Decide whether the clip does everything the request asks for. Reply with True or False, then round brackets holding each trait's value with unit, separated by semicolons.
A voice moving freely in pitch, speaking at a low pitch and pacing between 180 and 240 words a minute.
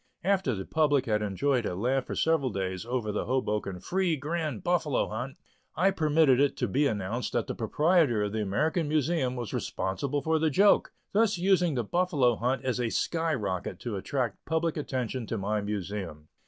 True (7.0 semitones; 130 Hz; 185 wpm)